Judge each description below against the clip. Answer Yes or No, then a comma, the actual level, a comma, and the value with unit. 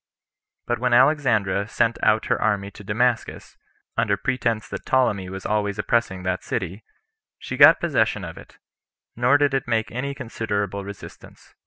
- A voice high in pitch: No, low, 110 Hz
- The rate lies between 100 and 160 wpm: Yes, average, 155 wpm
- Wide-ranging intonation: No, average, 3.4 semitones